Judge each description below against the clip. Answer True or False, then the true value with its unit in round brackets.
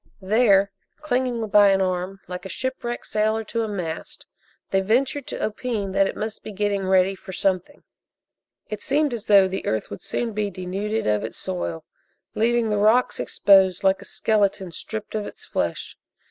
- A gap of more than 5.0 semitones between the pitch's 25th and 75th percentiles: False (2.8 semitones)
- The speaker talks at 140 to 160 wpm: False (175 wpm)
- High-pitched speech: True (205 Hz)